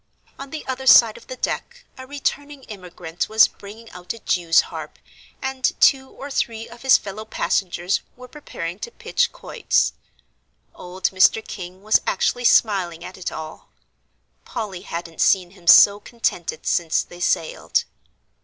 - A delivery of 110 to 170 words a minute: Yes, average, 155 wpm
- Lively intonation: Yes, wide, 6.4 semitones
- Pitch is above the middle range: Yes, high, 210 Hz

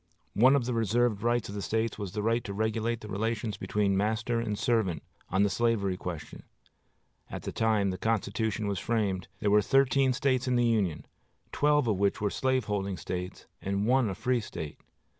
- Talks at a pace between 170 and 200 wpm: Yes, average, 190 wpm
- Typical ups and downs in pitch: Yes, average, 3.0 semitones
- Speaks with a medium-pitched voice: No, low, 110 Hz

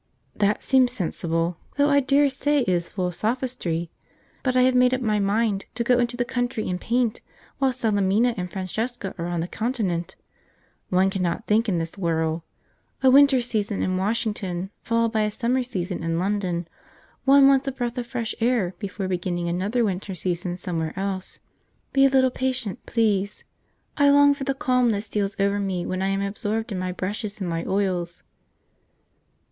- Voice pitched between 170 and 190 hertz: No, high, 210 Hz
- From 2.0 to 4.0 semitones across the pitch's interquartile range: No, average, 5.3 semitones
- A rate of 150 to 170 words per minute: No, average, 185 wpm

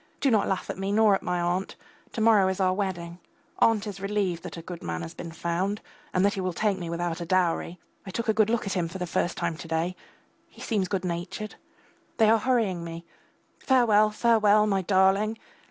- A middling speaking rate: No, fast, 220 wpm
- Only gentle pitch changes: No, average, 3.5 semitones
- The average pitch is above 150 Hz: Yes, high, 190 Hz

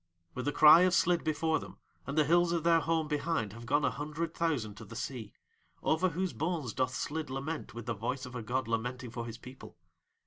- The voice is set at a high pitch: No, medium, 140 Hz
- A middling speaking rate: No, fast, 220 wpm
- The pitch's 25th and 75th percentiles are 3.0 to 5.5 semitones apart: Yes, average, 5.2 semitones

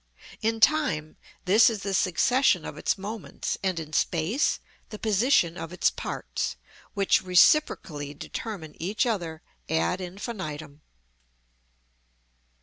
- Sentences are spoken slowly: Yes, slow, 115 wpm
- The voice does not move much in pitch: No, wide, 5.6 semitones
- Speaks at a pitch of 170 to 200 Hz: Yes, medium, 185 Hz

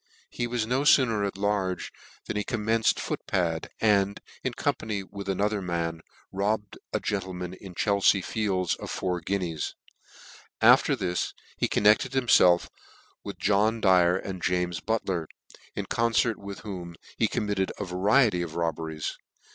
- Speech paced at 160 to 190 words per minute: No, average, 145 wpm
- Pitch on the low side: Yes, low, 100 Hz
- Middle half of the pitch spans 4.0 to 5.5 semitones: No, average, 3.0 semitones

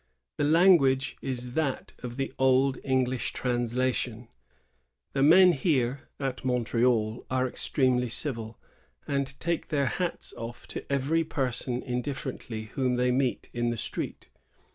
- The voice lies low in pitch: Yes, low, 130 Hz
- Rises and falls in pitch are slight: Yes, narrow, 2.2 semitones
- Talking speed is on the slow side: Yes, slow, 130 wpm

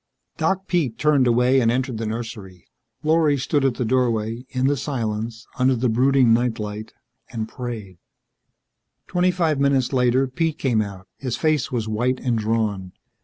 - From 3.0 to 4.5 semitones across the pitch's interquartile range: Yes, average, 3.5 semitones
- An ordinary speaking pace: Yes, average, 165 wpm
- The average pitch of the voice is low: Yes, low, 125 Hz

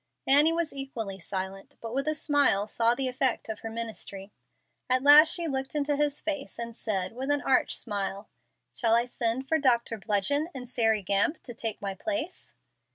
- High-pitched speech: Yes, high, 245 Hz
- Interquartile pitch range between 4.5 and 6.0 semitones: Yes, average, 4.8 semitones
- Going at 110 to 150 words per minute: No, average, 185 wpm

